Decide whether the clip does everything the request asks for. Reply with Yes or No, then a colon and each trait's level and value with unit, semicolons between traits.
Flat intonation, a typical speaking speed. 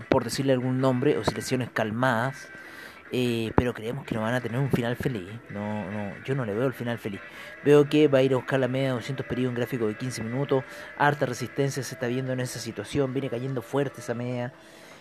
No: narrow, 2.3 semitones; fast, 230 wpm